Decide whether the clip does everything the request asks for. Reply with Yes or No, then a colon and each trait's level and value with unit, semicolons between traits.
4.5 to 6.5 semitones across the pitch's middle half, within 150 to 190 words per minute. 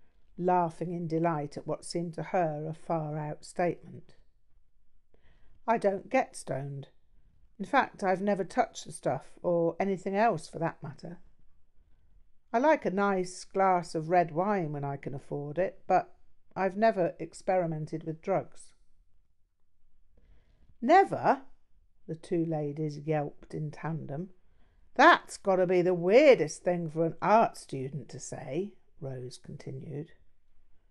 No: average, 4.8 semitones; slow, 135 wpm